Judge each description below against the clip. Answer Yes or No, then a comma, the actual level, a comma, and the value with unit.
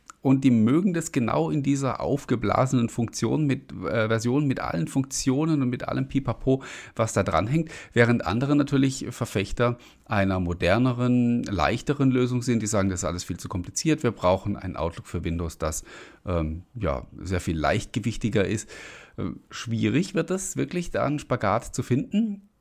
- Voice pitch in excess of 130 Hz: No, low, 120 Hz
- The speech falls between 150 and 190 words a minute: Yes, average, 165 wpm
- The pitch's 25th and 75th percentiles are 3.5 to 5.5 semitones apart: Yes, average, 5.1 semitones